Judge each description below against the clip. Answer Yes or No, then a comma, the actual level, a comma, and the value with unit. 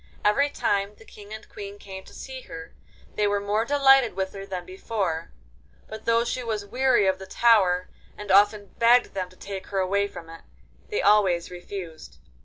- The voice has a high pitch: Yes, high, 200 Hz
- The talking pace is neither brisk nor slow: Yes, average, 190 wpm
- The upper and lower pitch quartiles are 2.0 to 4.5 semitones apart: Yes, average, 2.8 semitones